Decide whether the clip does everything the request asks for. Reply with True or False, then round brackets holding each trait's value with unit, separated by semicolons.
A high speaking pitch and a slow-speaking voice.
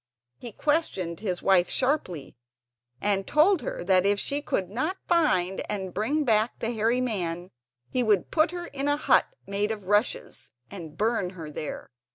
False (210 Hz; 170 wpm)